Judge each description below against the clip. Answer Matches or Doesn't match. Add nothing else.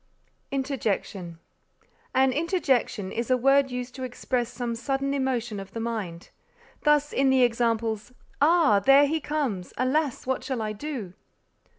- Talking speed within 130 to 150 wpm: Matches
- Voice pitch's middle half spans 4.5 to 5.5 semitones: Doesn't match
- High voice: Matches